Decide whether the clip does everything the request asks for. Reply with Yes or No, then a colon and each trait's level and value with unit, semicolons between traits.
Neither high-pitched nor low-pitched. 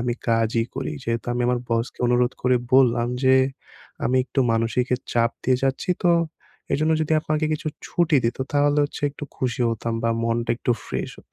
No: low, 125 Hz